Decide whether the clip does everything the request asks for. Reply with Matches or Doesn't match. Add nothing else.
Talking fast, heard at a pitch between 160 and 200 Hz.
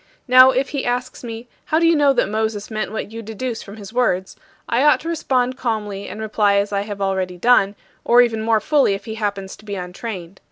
Doesn't match